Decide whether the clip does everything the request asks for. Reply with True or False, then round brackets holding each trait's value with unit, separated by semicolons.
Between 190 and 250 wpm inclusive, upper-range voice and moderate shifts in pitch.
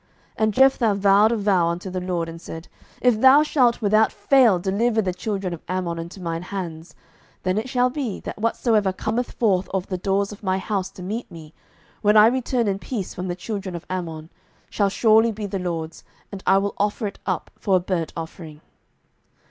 True (205 wpm; 195 Hz; 3.4 semitones)